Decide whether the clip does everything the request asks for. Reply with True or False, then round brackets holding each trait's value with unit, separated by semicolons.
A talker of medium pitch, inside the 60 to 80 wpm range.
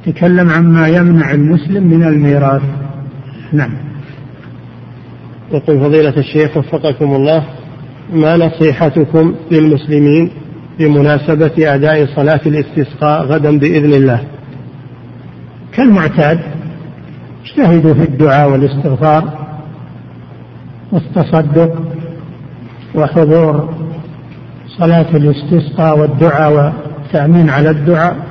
True (155 Hz; 75 wpm)